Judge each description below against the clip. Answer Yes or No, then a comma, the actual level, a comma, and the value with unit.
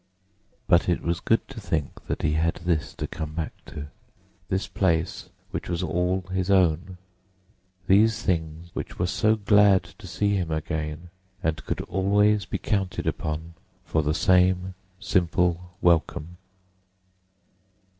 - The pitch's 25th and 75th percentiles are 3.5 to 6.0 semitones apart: No, average, 2.9 semitones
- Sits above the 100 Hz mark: No, very low, 90 Hz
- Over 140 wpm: No, slow, 135 wpm